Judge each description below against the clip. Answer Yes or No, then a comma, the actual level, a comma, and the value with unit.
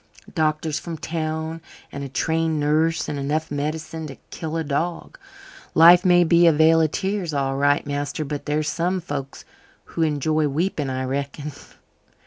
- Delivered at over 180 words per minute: No, average, 165 wpm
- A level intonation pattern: Yes, narrow, 2.2 semitones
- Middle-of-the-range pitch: Yes, medium, 155 Hz